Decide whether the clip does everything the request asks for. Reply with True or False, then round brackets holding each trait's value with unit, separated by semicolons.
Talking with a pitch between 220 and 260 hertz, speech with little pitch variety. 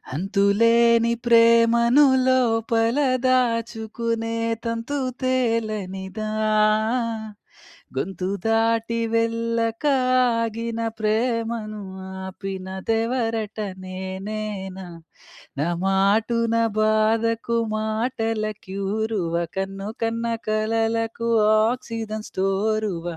True (225 Hz; 1.9 semitones)